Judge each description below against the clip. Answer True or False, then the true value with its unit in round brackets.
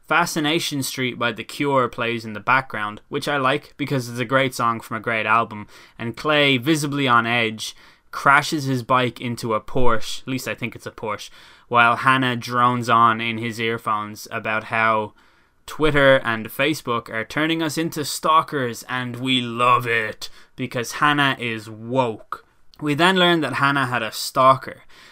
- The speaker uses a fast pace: False (170 wpm)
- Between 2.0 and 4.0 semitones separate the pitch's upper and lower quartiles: True (3.3 semitones)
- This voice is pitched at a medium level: False (125 Hz)